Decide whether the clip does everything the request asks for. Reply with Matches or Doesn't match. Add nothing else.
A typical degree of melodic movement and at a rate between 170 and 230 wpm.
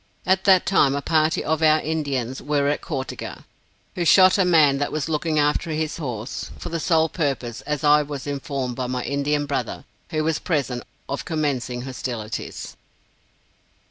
Matches